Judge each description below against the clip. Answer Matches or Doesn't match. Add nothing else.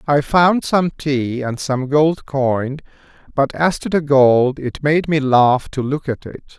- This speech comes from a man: Matches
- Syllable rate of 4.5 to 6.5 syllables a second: Doesn't match